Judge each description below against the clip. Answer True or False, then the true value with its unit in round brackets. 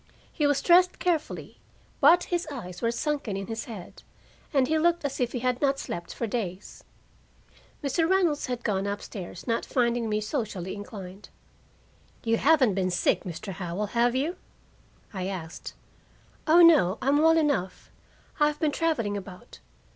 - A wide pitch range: True (7.2 semitones)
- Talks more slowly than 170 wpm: True (160 wpm)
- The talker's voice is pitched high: True (240 Hz)